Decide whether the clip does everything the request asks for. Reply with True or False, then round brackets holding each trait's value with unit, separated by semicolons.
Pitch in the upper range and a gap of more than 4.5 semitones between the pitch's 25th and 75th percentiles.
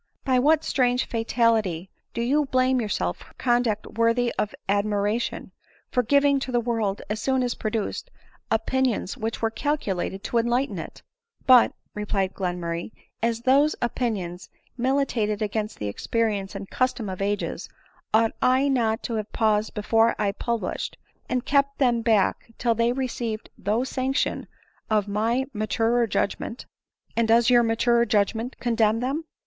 False (230 Hz; 3.0 semitones)